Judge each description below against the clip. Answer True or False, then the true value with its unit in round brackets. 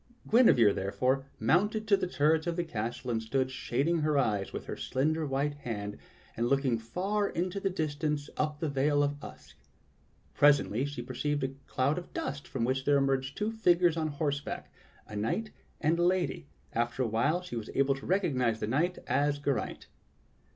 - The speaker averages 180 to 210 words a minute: True (190 wpm)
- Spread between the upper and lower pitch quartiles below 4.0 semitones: False (4.4 semitones)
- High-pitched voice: False (145 Hz)